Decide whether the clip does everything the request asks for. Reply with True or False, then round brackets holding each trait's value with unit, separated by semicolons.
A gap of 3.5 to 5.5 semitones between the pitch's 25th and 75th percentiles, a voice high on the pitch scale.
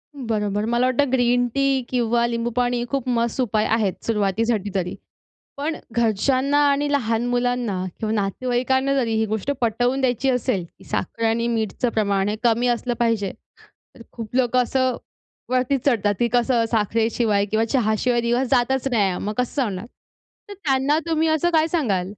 False (2.9 semitones; 240 Hz)